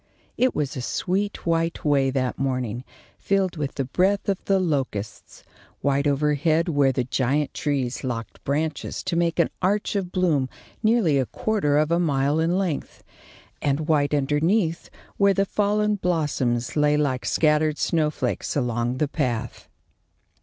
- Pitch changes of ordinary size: Yes, average, 4.6 semitones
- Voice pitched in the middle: Yes, medium, 150 Hz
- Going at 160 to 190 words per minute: No, average, 150 wpm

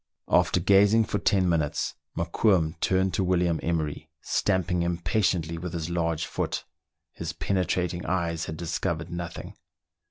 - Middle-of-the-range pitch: No, very low, 85 Hz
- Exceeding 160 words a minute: No, slow, 135 wpm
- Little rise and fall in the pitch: Yes, narrow, 2.0 semitones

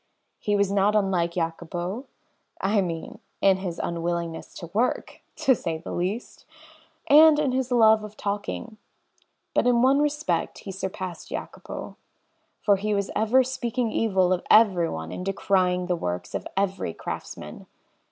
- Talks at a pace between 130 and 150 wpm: Yes, average, 145 wpm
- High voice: Yes, high, 195 Hz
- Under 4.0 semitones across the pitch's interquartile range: No, average, 4.3 semitones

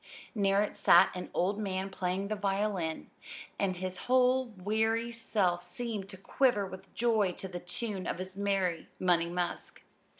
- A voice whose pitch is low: No, high, 195 Hz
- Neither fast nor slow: Yes, average, 160 wpm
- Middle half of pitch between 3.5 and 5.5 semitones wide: No, average, 2.8 semitones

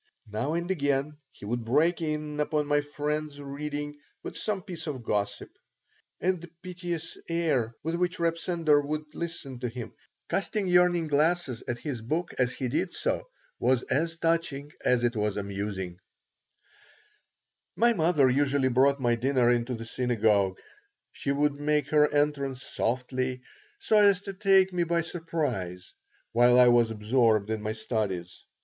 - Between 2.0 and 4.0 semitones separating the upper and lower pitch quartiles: No, wide, 5.5 semitones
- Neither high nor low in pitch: Yes, medium, 145 Hz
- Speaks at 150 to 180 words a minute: Yes, average, 155 wpm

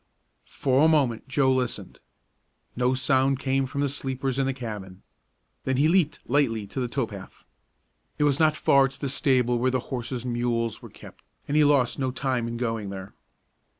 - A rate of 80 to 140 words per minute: No, average, 190 wpm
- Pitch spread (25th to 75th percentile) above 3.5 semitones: No, narrow, 2.5 semitones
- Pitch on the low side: Yes, low, 130 Hz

